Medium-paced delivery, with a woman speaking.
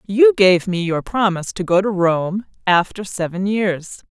Yes: average, 175 wpm; female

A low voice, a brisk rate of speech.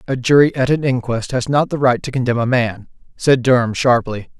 Yes: low, 125 Hz; fast, 220 wpm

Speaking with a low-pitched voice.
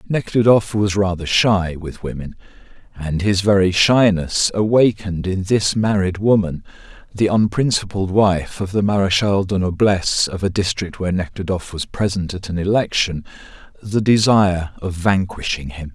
Yes: very low, 95 Hz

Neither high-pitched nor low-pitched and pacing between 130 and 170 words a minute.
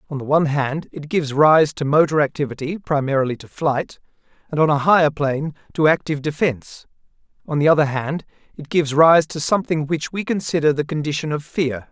No: medium, 150 Hz; average, 185 wpm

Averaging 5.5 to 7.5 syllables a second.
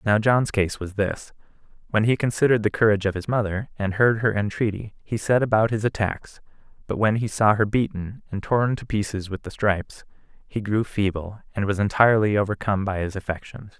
Yes: 5.6 syllables/s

